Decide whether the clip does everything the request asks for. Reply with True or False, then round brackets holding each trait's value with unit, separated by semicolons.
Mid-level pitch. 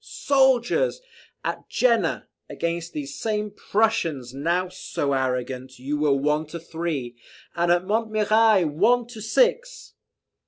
True (175 Hz)